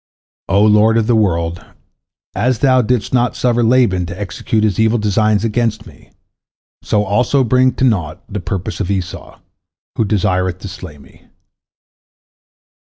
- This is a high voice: No, low, 105 Hz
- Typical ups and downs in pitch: Yes, average, 3.8 semitones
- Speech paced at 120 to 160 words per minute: Yes, average, 150 wpm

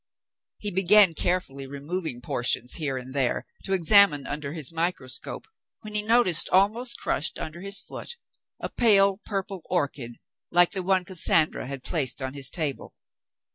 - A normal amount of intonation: No, wide, 5.9 semitones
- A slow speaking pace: No, average, 150 wpm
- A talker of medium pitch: Yes, medium, 170 Hz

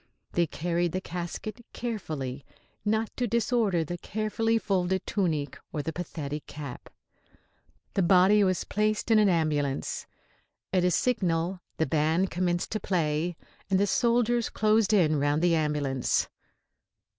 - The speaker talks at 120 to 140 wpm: Yes, slow, 135 wpm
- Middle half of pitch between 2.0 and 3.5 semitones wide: No, average, 5.2 semitones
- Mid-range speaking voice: Yes, medium, 180 Hz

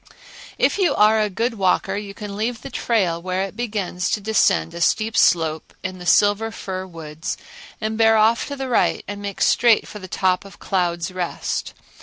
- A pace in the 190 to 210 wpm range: Yes, average, 195 wpm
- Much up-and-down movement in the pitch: No, average, 3.3 semitones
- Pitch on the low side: No, high, 200 Hz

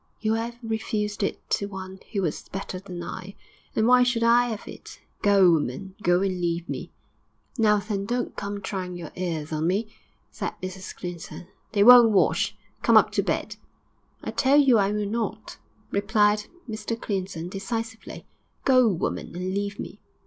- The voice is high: Yes, high, 200 Hz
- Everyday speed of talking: Yes, average, 170 wpm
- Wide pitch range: No, average, 3.4 semitones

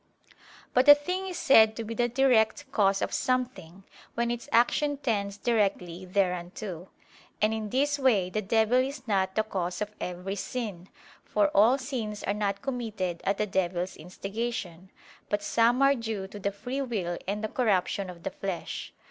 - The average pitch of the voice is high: Yes, high, 215 Hz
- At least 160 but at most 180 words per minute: Yes, average, 175 wpm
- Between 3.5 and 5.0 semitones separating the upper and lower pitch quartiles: Yes, average, 4.4 semitones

